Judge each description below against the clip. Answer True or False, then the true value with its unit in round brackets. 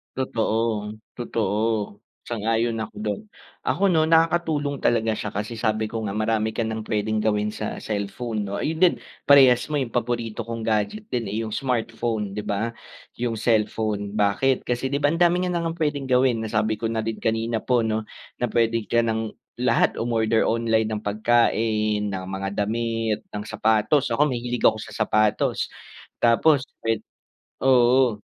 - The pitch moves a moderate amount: False (2.2 semitones)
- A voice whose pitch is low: True (115 Hz)